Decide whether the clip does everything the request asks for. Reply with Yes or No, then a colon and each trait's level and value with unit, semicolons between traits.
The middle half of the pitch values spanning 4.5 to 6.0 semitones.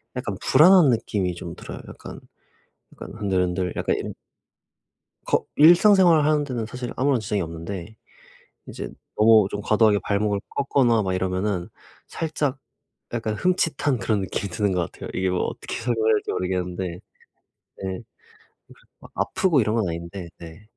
Yes: wide, 5.6 semitones